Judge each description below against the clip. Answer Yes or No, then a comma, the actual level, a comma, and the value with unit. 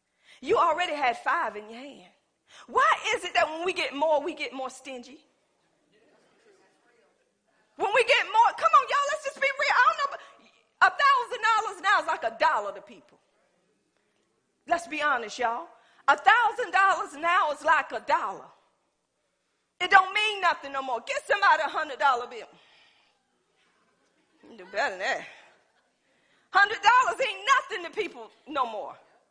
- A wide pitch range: Yes, wide, 5.8 semitones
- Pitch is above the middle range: Yes, very high, 320 Hz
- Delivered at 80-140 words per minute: No, average, 160 wpm